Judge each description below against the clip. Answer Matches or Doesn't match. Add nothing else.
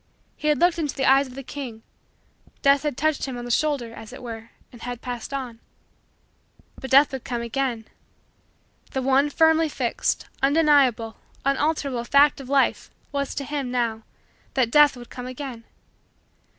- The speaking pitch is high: Matches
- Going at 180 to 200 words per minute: Doesn't match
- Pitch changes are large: Doesn't match